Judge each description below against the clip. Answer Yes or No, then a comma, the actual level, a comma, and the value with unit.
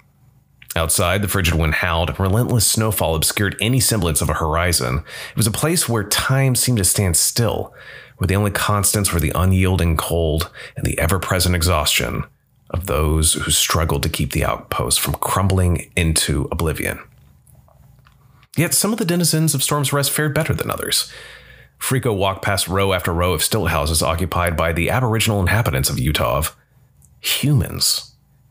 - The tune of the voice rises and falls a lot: Yes, wide, 7.4 semitones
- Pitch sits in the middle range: No, very low, 95 Hz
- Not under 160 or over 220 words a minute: Yes, average, 165 wpm